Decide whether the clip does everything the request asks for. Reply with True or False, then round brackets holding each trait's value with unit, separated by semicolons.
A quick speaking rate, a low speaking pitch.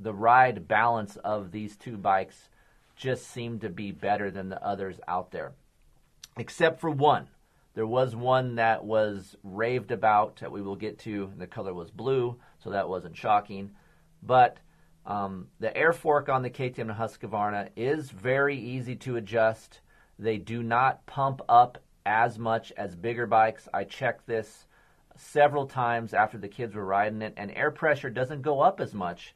False (170 wpm; 115 Hz)